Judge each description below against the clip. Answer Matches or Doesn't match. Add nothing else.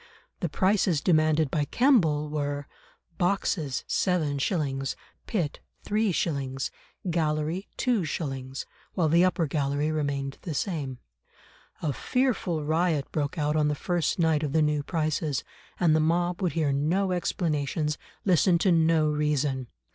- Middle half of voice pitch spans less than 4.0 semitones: Matches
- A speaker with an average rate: Doesn't match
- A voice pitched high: Doesn't match